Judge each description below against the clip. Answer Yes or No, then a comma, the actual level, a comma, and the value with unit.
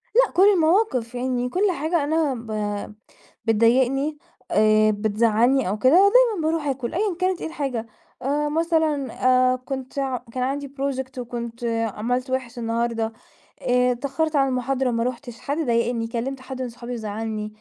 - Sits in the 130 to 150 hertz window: No, very high, 255 Hz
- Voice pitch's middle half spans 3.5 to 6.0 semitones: Yes, average, 3.9 semitones